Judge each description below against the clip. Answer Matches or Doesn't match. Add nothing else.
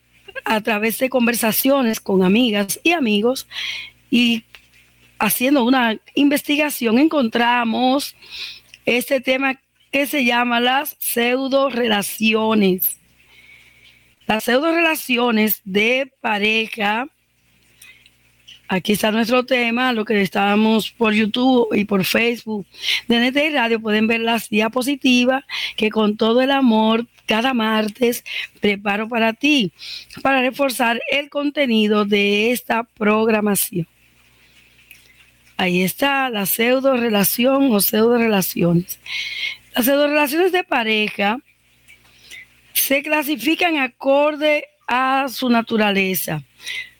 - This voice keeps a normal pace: Doesn't match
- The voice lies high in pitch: Matches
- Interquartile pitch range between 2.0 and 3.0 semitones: Doesn't match